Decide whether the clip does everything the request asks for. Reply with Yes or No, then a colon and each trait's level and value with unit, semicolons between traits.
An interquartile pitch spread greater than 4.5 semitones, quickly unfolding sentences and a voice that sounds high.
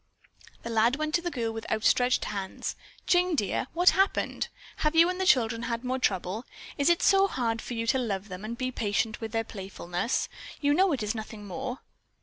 Yes: average, 5.3 semitones; fast, 210 wpm; high, 235 Hz